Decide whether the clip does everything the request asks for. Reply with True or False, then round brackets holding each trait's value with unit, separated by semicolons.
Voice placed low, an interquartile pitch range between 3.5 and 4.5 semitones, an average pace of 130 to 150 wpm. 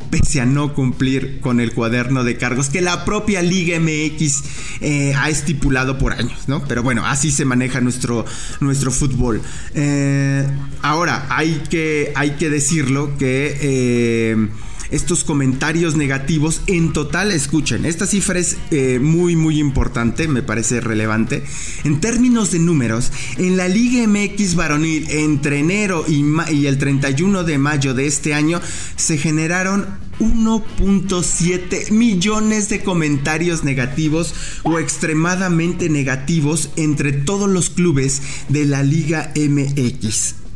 False (150 Hz; 4.1 semitones; 135 wpm)